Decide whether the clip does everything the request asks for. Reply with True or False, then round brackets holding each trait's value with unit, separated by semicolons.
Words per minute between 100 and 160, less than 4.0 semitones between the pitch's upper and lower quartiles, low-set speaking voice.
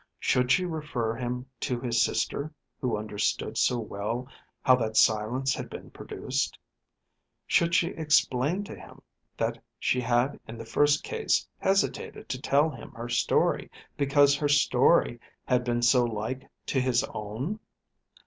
True (150 wpm; 3.6 semitones; 125 Hz)